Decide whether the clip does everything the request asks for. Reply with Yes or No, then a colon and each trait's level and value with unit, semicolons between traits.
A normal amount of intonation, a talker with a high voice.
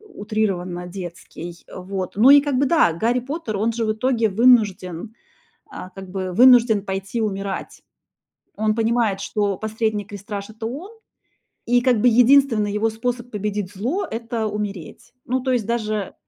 Yes: average, 3.5 semitones; high, 220 Hz